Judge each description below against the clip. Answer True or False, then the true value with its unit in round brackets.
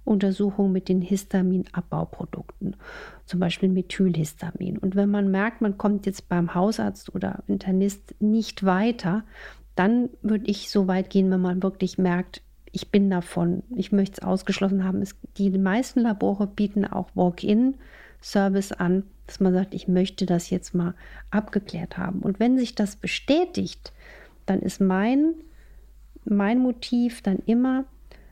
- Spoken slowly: False (145 wpm)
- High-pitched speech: True (195 Hz)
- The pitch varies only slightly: True (2.2 semitones)